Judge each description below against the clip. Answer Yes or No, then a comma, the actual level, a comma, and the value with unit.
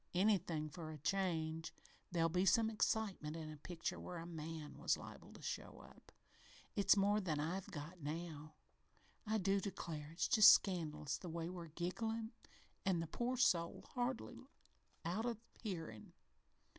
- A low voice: No, medium, 175 Hz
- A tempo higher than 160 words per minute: No, average, 155 wpm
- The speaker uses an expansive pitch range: No, average, 3.9 semitones